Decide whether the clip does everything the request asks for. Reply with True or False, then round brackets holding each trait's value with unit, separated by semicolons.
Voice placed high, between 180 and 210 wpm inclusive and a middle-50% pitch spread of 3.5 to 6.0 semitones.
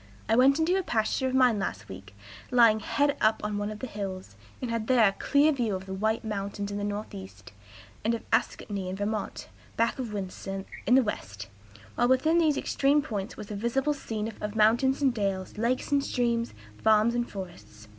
True (220 Hz; 200 wpm; 4.0 semitones)